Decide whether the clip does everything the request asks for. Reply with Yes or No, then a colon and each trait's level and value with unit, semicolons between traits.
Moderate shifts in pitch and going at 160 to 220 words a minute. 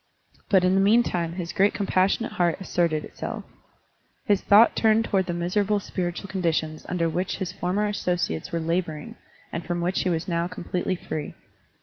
No: narrow, 2.3 semitones; average, 180 wpm